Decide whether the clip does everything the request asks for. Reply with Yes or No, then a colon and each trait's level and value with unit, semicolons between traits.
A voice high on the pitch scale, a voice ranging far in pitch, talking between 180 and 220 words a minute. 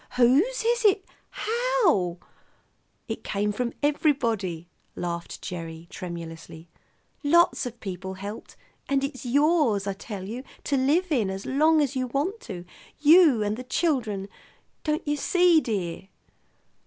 No: very high, 250 Hz; wide, 8.2 semitones; average, 140 wpm